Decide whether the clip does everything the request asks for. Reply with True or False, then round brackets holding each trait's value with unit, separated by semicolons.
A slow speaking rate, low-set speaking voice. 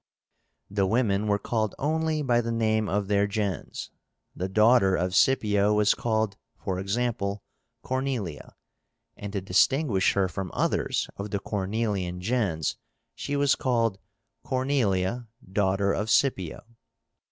True (130 wpm; 105 Hz)